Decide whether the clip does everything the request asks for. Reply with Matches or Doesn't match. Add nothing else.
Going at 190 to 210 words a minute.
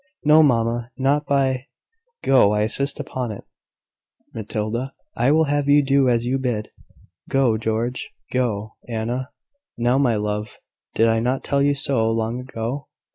Doesn't match